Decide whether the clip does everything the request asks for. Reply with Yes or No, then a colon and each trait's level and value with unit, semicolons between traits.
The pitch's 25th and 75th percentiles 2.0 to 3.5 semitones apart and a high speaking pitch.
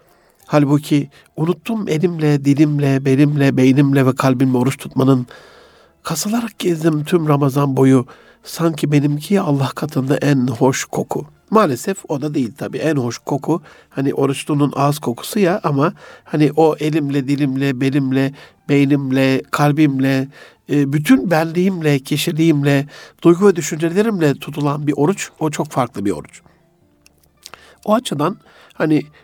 No: average, 2.9 semitones; medium, 145 Hz